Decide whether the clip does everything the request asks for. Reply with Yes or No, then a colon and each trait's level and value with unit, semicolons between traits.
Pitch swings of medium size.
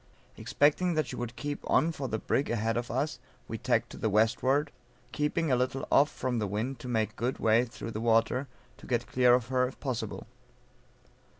Yes: average, 3.5 semitones